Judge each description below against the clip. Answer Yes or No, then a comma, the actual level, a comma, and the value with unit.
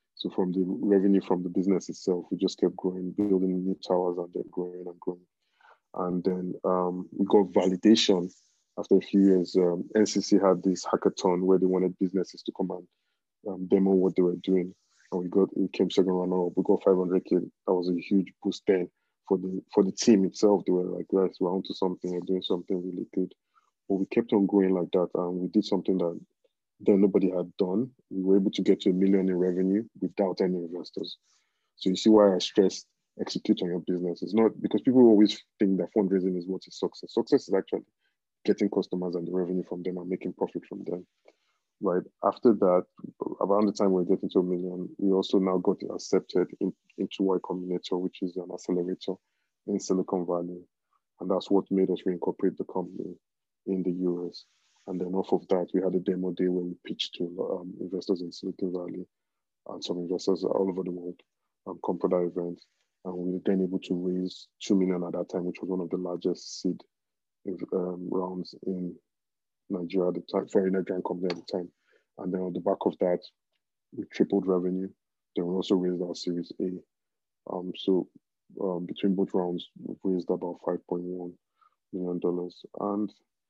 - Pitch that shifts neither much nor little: No, narrow, 1.1 semitones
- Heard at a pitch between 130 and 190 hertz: No, very low, 95 Hz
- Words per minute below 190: No, average, 200 wpm